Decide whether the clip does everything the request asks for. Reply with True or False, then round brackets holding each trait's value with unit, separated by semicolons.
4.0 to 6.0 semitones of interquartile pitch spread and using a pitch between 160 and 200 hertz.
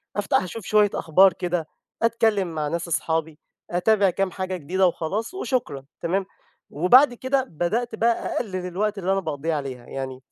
True (4.7 semitones; 185 Hz)